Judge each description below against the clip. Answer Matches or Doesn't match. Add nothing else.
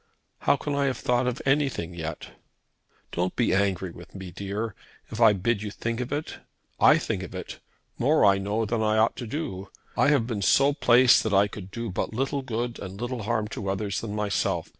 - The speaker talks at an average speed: Doesn't match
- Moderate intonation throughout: Matches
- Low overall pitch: Matches